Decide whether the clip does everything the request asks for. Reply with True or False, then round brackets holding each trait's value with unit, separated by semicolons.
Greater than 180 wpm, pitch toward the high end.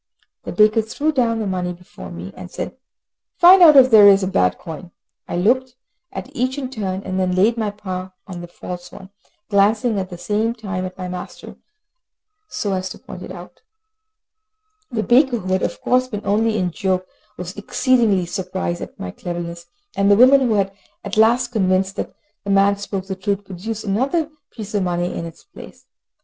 True (195 wpm; 200 Hz)